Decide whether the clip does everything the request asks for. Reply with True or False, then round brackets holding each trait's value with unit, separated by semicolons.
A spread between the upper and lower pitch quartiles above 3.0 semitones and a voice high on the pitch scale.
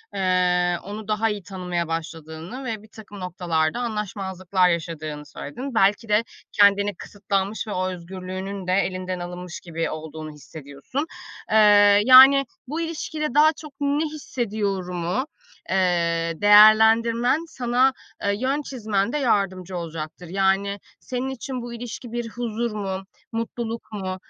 True (4.6 semitones; 200 Hz)